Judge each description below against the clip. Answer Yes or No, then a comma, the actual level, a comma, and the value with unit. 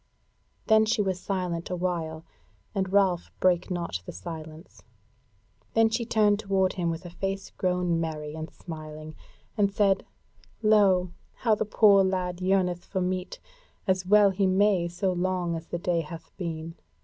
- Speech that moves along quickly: No, average, 160 wpm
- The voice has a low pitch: No, medium, 185 Hz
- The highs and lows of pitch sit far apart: No, narrow, 2.6 semitones